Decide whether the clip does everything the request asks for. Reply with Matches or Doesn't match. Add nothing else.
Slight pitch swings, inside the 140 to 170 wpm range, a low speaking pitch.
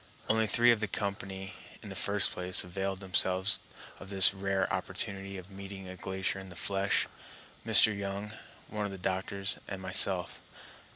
Matches